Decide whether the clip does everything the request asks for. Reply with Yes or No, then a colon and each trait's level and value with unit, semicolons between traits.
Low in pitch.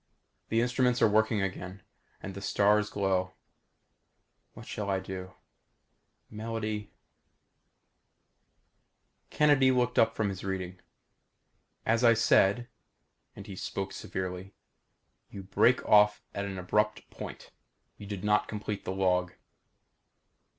Yes: low, 100 Hz